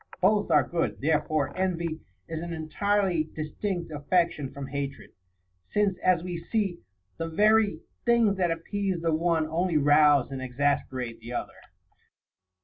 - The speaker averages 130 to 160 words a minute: Yes, average, 140 wpm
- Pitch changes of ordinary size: Yes, average, 4.0 semitones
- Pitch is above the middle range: No, medium, 165 Hz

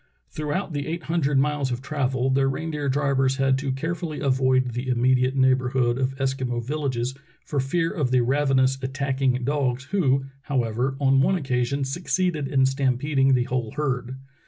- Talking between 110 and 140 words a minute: No, average, 155 wpm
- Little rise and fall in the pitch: Yes, narrow, 2.0 semitones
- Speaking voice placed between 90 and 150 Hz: Yes, low, 135 Hz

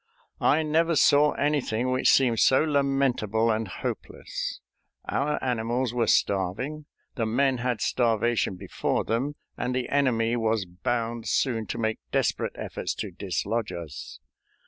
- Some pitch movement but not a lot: Yes, average, 3.7 semitones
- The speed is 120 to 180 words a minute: Yes, slow, 135 wpm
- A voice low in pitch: Yes, low, 120 Hz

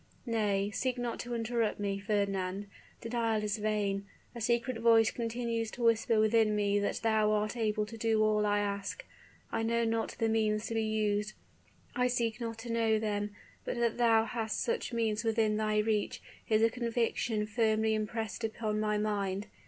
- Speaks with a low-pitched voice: No, high, 220 Hz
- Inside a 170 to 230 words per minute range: Yes, average, 175 wpm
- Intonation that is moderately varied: No, narrow, 1.5 semitones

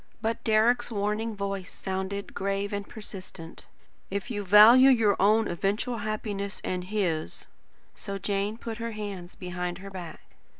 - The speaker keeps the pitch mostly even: Yes, narrow, 2.3 semitones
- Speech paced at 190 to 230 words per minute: No, average, 145 wpm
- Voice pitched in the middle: No, high, 200 Hz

